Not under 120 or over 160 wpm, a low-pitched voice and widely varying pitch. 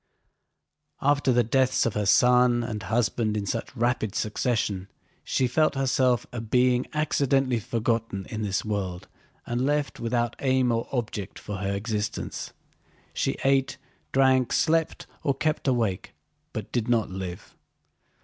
No: average, 140 wpm; low, 120 Hz; average, 3.5 semitones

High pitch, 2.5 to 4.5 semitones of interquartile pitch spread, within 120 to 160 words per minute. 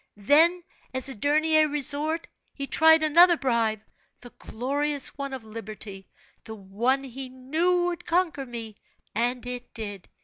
No: very high, 265 Hz; average, 5.2 semitones; average, 140 wpm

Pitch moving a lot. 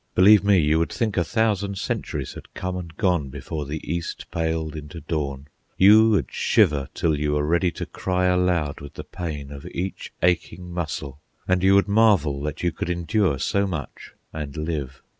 No: average, 3.9 semitones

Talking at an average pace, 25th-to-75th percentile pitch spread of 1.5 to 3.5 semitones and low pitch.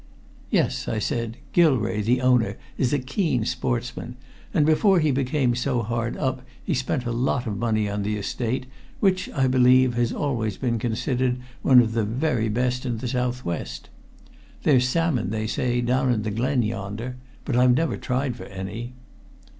Yes: average, 170 wpm; narrow, 2.4 semitones; low, 125 Hz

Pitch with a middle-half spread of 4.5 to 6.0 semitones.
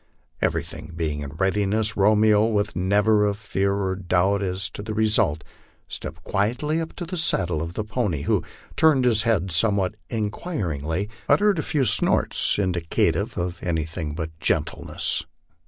No: average, 4.1 semitones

